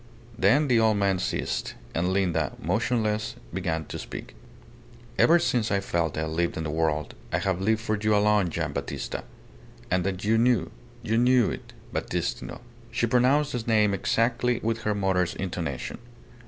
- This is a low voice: Yes, low, 100 Hz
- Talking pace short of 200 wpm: Yes, average, 165 wpm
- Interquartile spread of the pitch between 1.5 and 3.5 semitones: No, average, 4.5 semitones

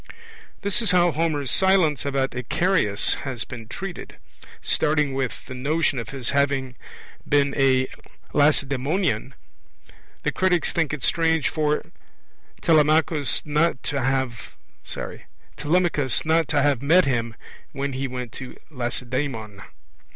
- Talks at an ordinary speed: No, slow, 110 wpm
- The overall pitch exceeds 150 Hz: No, medium, 140 Hz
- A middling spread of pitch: Yes, average, 3.7 semitones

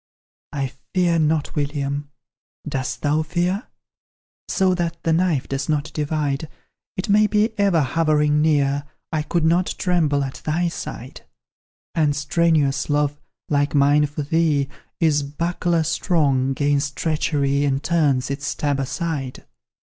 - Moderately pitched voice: Yes, medium, 150 Hz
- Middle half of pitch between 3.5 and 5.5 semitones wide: No, average, 2.8 semitones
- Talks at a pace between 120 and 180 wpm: Yes, slow, 135 wpm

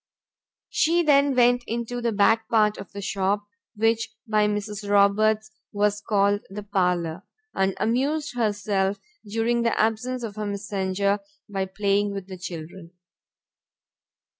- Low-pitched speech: No, high, 210 Hz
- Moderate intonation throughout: No, narrow, 2.3 semitones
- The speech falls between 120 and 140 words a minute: Yes, slow, 135 wpm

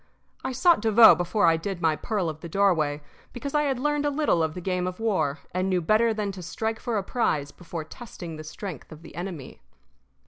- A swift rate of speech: Yes, fast, 220 wpm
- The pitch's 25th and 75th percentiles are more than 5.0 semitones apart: Yes, wide, 5.4 semitones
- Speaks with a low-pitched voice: No, medium, 185 Hz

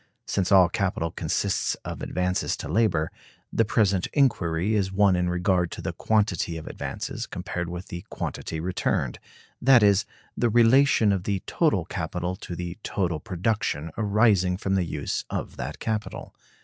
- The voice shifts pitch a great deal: No, average, 3.3 semitones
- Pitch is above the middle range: No, very low, 95 Hz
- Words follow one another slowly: No, average, 160 wpm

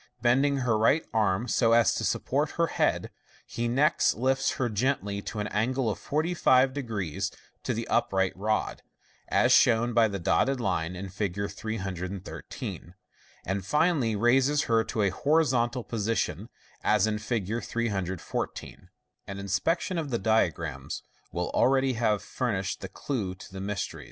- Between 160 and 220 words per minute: No, average, 145 wpm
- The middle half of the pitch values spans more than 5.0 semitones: No, average, 4.7 semitones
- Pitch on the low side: Yes, low, 110 Hz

